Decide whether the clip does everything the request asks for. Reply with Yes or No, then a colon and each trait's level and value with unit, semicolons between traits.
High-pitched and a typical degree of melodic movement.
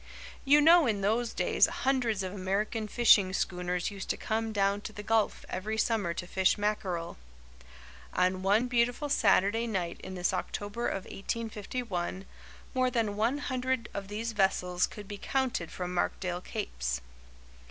Yes: high, 205 Hz; average, 3.7 semitones